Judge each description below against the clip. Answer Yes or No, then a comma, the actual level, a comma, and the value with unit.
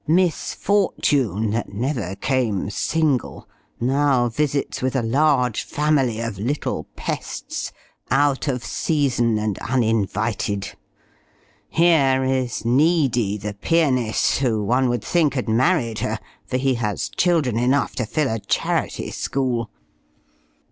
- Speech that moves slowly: Yes, slow, 120 wpm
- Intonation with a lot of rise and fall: No, average, 4.2 semitones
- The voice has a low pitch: Yes, low, 125 Hz